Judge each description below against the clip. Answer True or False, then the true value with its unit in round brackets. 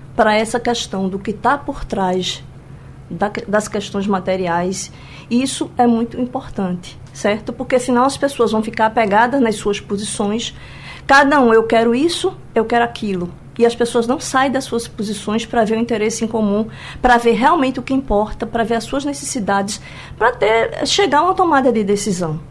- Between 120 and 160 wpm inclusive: False (180 wpm)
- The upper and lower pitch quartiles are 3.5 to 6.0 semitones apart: True (3.8 semitones)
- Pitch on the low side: False (225 Hz)